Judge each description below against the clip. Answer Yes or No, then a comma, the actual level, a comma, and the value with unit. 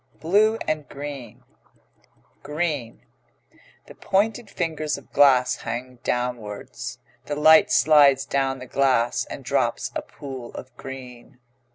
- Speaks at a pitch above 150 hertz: No, medium, 140 Hz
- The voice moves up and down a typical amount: Yes, average, 3.7 semitones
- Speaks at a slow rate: Yes, slow, 115 wpm